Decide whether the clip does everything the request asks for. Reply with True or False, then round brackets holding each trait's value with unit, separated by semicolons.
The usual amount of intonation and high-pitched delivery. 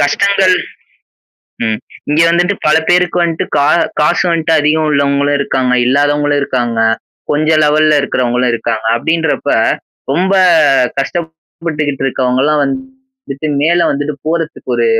False (3.3 semitones; 150 Hz)